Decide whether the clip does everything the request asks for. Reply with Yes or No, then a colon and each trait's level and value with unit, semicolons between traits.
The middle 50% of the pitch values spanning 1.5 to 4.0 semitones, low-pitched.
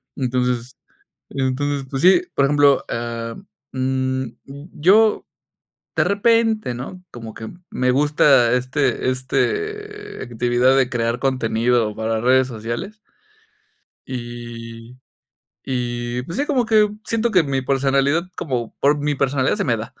Yes: average, 3.6 semitones; low, 130 Hz